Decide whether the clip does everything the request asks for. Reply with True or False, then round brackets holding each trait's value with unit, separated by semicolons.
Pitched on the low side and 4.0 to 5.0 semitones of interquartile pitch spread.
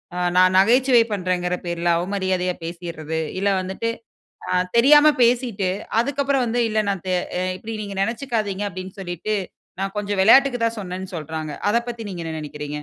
False (195 Hz; 4.5 semitones)